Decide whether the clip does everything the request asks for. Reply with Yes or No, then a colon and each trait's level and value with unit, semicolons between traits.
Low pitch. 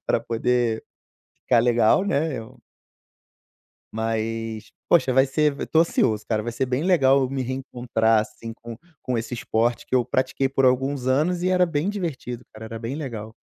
Yes: low, 125 Hz